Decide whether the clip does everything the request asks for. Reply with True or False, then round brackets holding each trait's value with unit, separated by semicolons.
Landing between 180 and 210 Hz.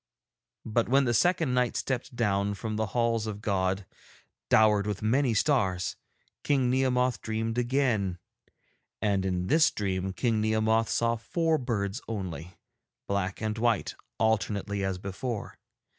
False (110 Hz)